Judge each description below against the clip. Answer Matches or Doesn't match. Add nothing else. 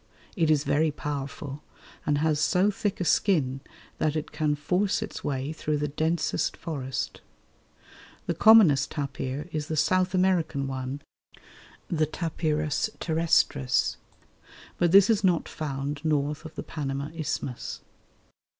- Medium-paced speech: Doesn't match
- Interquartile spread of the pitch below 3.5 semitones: Matches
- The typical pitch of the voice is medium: Matches